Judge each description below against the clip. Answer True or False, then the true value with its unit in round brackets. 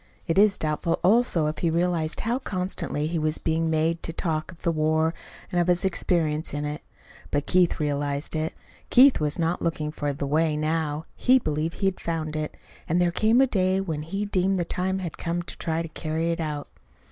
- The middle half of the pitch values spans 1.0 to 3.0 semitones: True (2.7 semitones)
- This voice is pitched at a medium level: True (165 Hz)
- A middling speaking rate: False (210 wpm)